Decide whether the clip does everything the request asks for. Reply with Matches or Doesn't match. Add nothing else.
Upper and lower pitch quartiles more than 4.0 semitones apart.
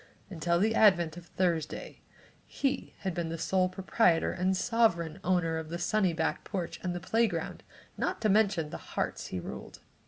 Doesn't match